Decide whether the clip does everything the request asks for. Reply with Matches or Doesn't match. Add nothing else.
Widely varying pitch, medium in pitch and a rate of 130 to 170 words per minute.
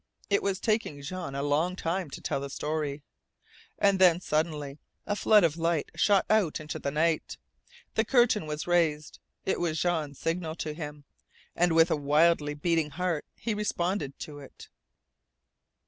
Doesn't match